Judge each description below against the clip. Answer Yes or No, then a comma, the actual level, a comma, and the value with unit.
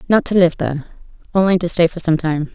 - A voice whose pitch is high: No, medium, 170 Hz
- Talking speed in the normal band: No, fast, 235 wpm